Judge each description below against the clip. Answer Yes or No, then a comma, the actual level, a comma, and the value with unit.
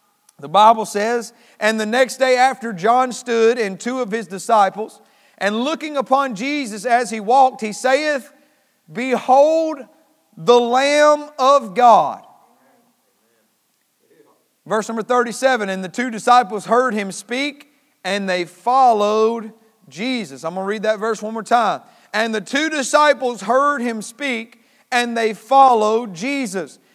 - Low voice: No, high, 235 Hz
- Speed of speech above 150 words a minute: No, average, 140 wpm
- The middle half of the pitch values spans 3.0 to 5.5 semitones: Yes, average, 3.5 semitones